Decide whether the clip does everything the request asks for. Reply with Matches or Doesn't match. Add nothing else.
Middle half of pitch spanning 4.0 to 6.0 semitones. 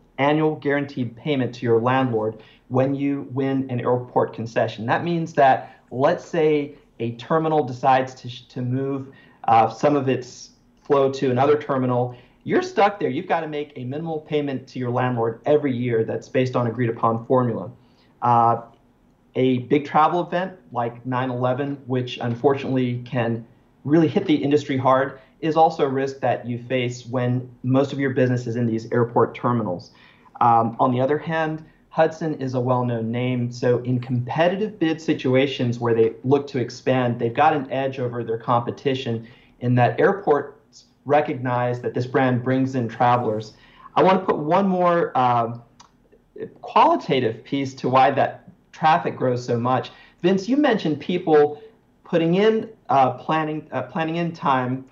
Doesn't match